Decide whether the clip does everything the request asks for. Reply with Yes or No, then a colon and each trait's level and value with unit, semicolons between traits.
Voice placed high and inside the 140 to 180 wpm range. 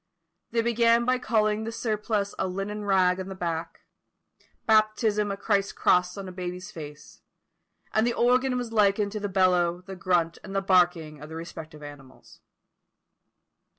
Yes: high, 195 Hz; average, 160 wpm